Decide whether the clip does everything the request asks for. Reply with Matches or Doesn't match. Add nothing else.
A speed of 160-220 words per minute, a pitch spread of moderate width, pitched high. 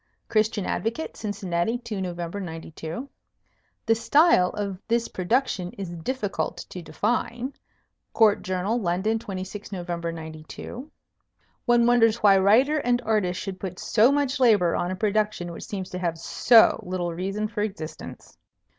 Doesn't match